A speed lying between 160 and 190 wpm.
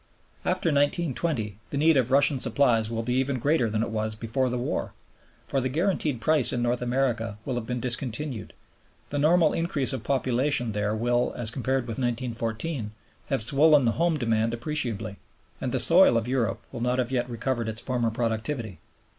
Yes: average, 180 wpm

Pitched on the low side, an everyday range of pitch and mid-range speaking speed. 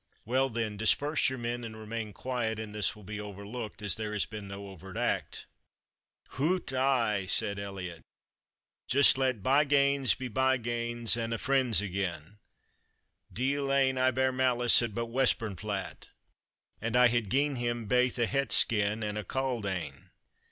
Yes: low, 115 Hz; average, 3.8 semitones; average, 160 wpm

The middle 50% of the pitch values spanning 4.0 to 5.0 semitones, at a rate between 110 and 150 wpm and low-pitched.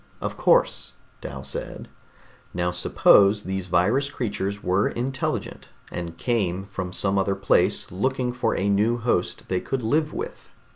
Yes: average, 4.7 semitones; average, 145 wpm; low, 100 Hz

